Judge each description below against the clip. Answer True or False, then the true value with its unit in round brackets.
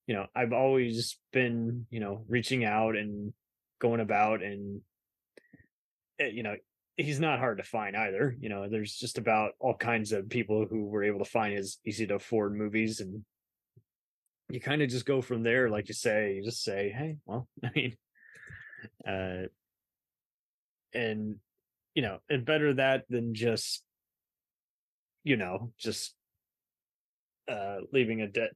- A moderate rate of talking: True (155 wpm)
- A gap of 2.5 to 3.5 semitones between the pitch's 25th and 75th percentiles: True (3.0 semitones)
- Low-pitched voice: True (110 Hz)